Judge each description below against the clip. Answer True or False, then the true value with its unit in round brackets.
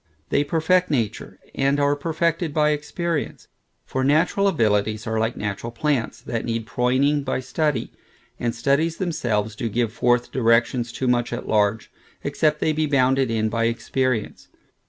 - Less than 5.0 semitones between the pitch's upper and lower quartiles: True (4.5 semitones)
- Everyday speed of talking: True (155 wpm)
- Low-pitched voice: True (130 Hz)